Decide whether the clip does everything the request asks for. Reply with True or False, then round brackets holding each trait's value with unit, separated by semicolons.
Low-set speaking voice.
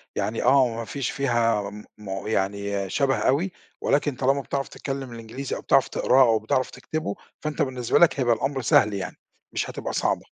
True (120 Hz)